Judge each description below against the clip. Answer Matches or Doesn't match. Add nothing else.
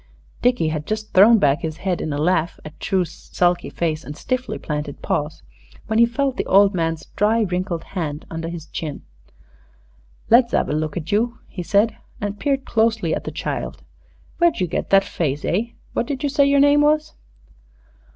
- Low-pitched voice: Doesn't match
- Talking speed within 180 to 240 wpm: Matches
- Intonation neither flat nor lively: Doesn't match